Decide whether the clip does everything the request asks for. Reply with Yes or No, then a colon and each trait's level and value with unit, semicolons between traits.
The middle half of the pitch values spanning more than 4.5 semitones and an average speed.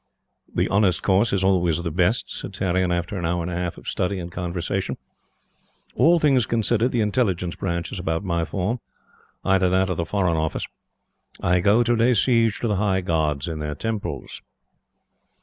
No: average, 3.5 semitones; average, 185 wpm